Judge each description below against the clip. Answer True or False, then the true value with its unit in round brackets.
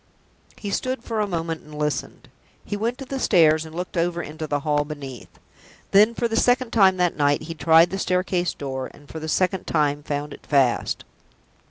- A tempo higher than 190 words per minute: True (200 wpm)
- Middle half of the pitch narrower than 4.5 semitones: False (4.8 semitones)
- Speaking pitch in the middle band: True (165 Hz)